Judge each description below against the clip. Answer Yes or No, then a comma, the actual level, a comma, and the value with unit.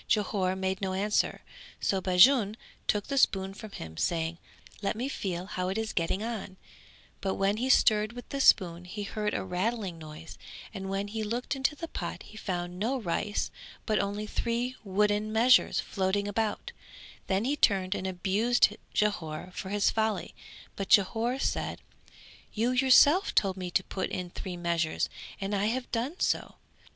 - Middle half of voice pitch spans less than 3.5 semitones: Yes, average, 3.1 semitones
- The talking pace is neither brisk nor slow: Yes, average, 170 wpm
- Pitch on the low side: No, high, 205 Hz